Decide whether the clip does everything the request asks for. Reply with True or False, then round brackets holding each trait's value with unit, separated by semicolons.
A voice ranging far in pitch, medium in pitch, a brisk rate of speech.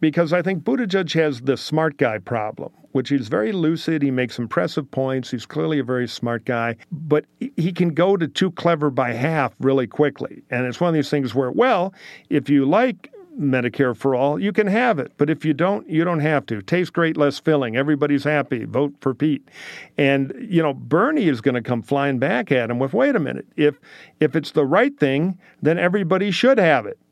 False (4.3 semitones; 150 Hz; 215 wpm)